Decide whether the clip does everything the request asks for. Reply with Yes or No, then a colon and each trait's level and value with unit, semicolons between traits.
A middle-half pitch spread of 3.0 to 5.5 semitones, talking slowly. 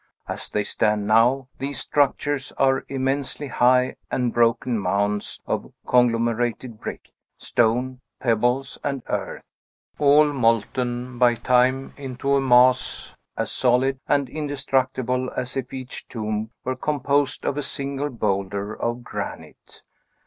No: narrow, 2.5 semitones; slow, 125 wpm